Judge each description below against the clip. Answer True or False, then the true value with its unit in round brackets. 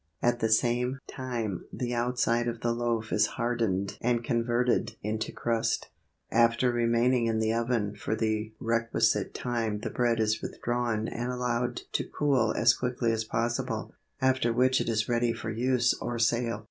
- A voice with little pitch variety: True (1.4 semitones)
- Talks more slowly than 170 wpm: True (160 wpm)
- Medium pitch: False (115 Hz)